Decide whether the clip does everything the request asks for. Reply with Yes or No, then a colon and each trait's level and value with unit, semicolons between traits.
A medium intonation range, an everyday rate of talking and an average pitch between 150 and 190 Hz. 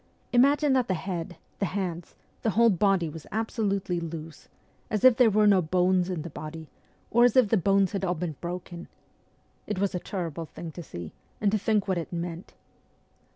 Yes: average, 3.7 semitones; average, 195 wpm; medium, 185 Hz